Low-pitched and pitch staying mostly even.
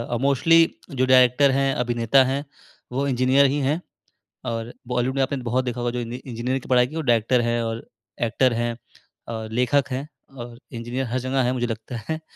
Yes: low, 125 Hz; narrow, 2.3 semitones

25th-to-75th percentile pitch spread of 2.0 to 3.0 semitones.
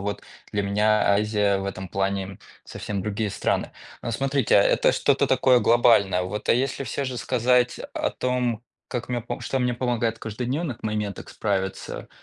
No: average, 3.7 semitones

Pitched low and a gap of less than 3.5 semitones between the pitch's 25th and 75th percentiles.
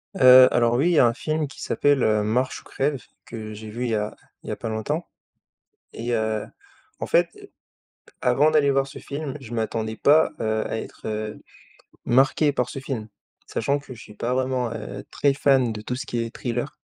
No: low, 125 Hz; average, 3.8 semitones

